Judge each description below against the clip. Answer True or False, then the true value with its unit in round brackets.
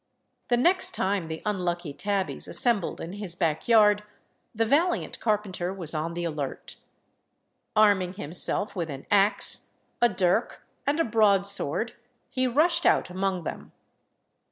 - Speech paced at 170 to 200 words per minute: False (135 wpm)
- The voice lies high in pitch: True (195 Hz)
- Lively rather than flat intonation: False (4.2 semitones)